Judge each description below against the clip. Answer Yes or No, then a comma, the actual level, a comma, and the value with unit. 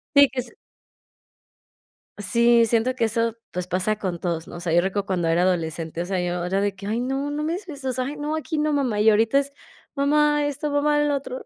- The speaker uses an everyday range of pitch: No, wide, 7.4 semitones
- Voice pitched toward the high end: Yes, high, 235 Hz